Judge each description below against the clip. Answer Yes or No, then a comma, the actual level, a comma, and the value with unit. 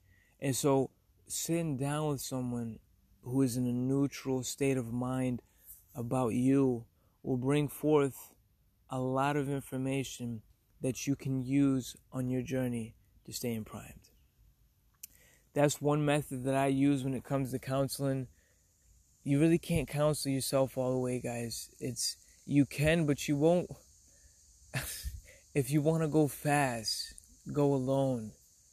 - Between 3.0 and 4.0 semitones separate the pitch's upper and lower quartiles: Yes, average, 3.7 semitones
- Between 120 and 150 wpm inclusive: Yes, average, 140 wpm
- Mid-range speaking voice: No, low, 130 Hz